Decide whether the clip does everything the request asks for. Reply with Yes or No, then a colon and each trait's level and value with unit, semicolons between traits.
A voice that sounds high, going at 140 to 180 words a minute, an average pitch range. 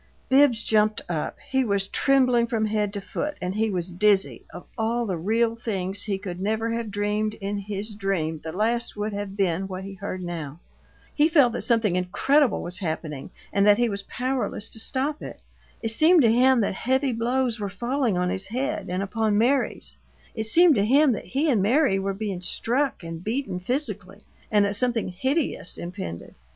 No: high, 210 Hz; average, 190 wpm; average, 4.0 semitones